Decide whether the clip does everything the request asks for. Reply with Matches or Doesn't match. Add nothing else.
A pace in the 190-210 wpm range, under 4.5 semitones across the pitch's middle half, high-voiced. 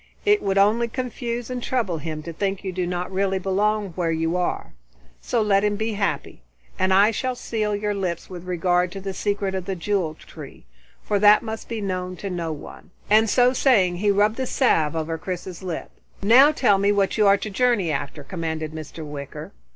Matches